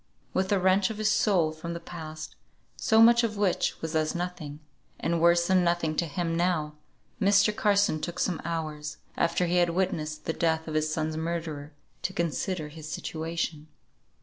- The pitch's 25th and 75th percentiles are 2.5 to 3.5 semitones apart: Yes, average, 2.8 semitones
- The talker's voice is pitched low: No, medium, 170 Hz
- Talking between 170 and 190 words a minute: Yes, average, 175 wpm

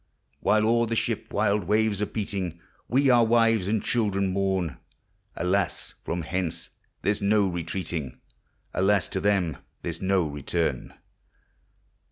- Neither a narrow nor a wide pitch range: Yes, average, 3.5 semitones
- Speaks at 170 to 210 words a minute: No, average, 140 wpm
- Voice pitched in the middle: No, low, 100 Hz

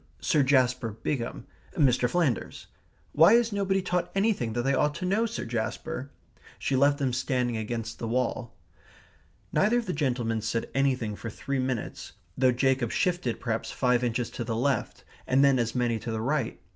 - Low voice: Yes, low, 130 Hz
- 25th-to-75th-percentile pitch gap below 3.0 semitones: No, average, 4.1 semitones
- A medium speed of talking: Yes, average, 175 wpm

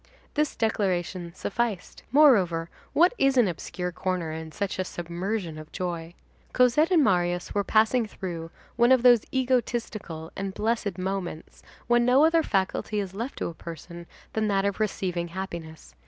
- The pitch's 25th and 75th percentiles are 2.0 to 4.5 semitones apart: No, wide, 5.4 semitones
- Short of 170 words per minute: Yes, average, 155 wpm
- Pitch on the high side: Yes, high, 195 Hz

